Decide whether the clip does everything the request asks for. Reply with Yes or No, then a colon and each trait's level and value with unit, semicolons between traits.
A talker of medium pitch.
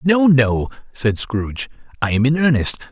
No: low, 130 Hz